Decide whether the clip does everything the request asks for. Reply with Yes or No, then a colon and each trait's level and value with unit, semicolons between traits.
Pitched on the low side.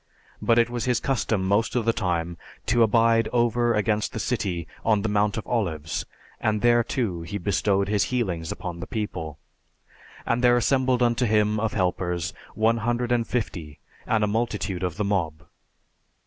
Yes: low, 105 Hz